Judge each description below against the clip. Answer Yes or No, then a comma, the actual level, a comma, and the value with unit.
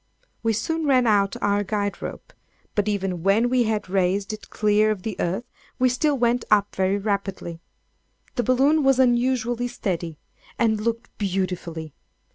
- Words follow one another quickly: No, average, 155 wpm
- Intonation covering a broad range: No, average, 3.8 semitones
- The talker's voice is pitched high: Yes, high, 215 Hz